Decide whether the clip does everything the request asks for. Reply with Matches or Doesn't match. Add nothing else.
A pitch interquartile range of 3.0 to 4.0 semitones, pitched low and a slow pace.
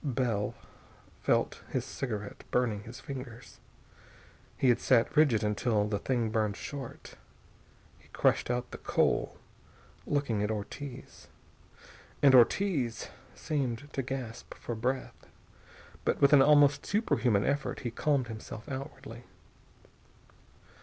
Matches